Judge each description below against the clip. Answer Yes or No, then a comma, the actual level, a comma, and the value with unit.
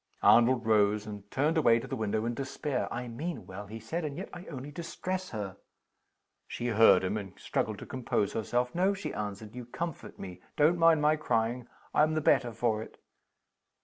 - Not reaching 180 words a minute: No, average, 190 wpm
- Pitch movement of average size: No, wide, 6.0 semitones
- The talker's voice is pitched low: Yes, low, 120 Hz